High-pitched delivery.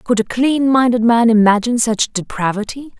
Yes: high, 235 Hz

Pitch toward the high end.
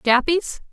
Yes: very high, 295 Hz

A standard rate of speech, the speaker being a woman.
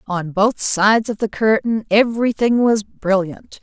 Yes: average, 150 wpm; female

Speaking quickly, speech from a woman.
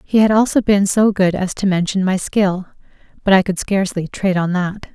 Yes: fast, 220 wpm; female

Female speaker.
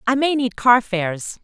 Yes: female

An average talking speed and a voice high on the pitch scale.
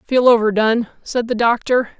Yes: average, 150 wpm; high, 230 Hz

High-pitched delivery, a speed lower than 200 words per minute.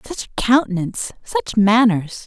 Yes: high, 225 Hz; slow, 135 wpm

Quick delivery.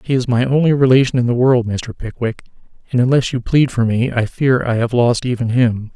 Yes: fast, 230 wpm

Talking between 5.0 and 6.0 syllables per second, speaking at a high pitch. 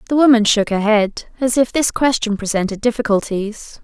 Yes: 5.1 syllables/s; high, 225 Hz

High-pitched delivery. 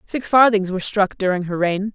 Yes: high, 200 Hz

